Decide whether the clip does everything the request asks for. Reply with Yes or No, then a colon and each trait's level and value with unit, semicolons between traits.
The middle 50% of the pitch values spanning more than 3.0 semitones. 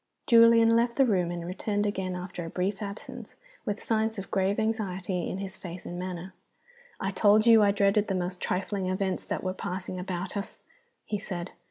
No: narrow, 2.4 semitones